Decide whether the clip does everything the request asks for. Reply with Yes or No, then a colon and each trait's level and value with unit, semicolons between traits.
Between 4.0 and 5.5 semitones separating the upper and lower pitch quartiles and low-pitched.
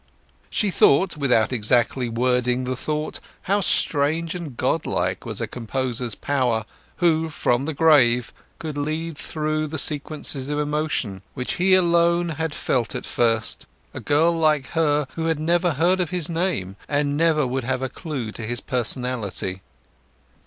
No: average, 4.5 semitones; medium, 145 Hz